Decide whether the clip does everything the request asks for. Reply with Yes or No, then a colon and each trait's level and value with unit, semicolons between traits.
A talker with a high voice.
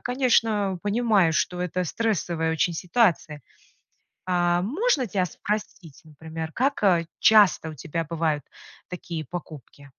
No: medium, 175 Hz